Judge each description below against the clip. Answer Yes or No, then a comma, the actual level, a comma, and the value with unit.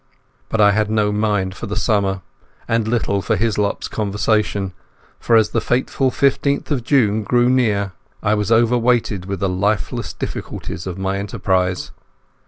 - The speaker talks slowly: No, average, 155 wpm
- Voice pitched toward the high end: No, low, 105 Hz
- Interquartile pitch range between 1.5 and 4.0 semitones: Yes, average, 2.7 semitones